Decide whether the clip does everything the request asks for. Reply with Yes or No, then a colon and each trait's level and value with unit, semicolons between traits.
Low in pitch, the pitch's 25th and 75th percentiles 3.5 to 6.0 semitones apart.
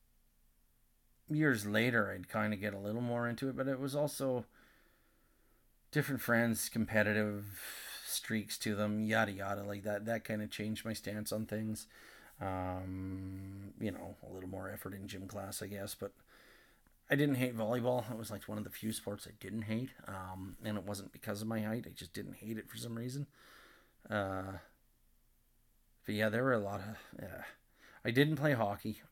No: low, 105 Hz; average, 2.8 semitones